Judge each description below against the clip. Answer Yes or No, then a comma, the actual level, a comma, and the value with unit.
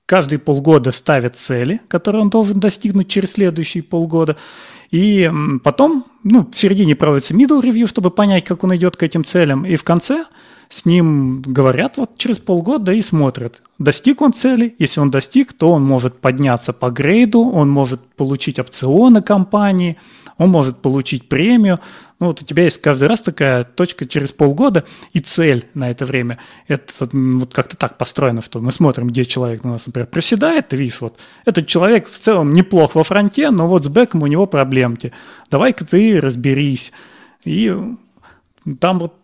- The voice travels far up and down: Yes, wide, 7.0 semitones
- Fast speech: Yes, fast, 170 wpm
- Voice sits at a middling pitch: Yes, medium, 165 Hz